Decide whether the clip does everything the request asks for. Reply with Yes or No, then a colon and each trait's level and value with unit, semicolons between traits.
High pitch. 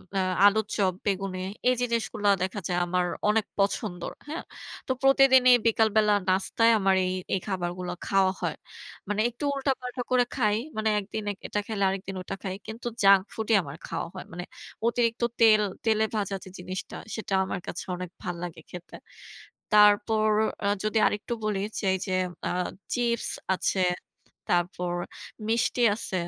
Yes: high, 205 Hz